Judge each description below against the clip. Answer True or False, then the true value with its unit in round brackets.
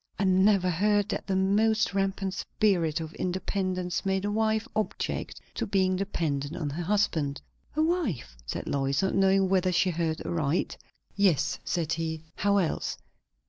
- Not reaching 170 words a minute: True (155 wpm)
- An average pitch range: True (3.4 semitones)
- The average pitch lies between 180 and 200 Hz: True (190 Hz)